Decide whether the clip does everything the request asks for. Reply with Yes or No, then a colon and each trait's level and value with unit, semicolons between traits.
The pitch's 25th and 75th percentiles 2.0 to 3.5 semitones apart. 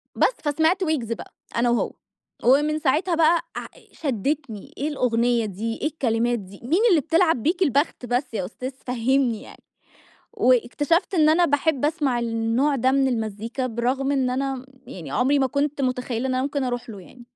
No: average, 4.0 semitones